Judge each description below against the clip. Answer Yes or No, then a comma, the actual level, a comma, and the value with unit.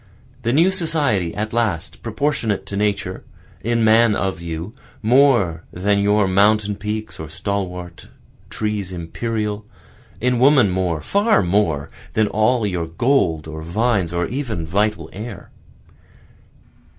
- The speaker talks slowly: Yes, slow, 125 wpm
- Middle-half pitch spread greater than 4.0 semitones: Yes, average, 4.5 semitones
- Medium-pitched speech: No, low, 105 Hz